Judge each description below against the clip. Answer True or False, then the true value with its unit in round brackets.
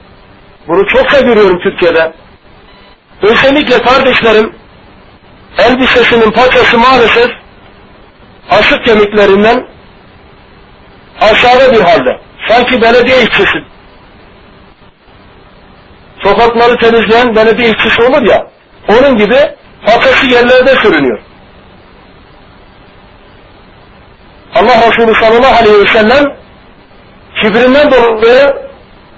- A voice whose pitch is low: False (240 Hz)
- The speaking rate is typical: False (75 wpm)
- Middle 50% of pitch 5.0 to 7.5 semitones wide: False (2.5 semitones)